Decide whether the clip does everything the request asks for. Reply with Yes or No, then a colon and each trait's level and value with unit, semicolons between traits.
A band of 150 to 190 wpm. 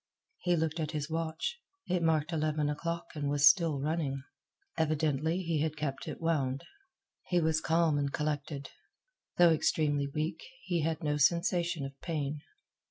Yes: average, 155 wpm